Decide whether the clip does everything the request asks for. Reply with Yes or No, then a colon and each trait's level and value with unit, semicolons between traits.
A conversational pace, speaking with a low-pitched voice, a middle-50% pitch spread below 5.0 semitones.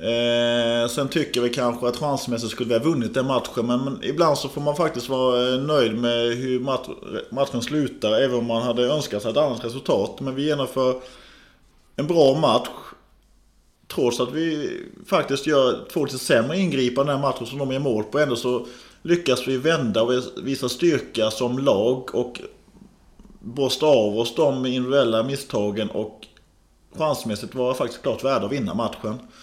Yes: average, 170 wpm; low, 125 Hz; average, 2.7 semitones